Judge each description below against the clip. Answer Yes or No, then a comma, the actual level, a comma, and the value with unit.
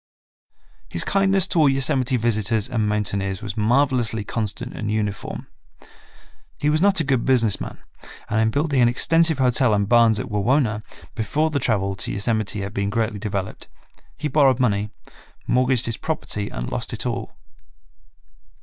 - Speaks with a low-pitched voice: Yes, low, 115 Hz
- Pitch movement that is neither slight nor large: Yes, average, 4.3 semitones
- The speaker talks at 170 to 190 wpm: No, average, 160 wpm